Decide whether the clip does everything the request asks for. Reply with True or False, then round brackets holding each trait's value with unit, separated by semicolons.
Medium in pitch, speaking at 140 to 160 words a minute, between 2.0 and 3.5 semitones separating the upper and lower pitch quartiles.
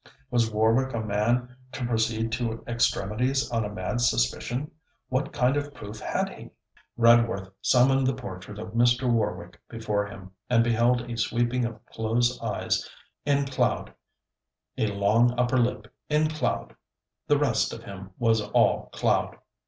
False (115 Hz; 150 wpm; 2.4 semitones)